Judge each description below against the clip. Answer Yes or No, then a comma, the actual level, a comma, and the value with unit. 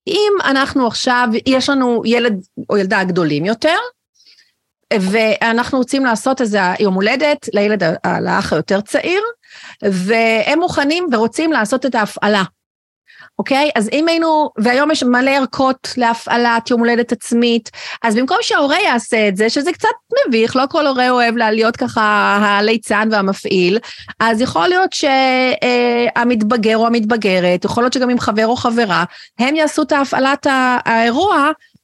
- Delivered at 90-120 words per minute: No, average, 145 wpm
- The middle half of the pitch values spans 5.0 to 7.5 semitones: No, average, 4.0 semitones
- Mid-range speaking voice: No, high, 240 Hz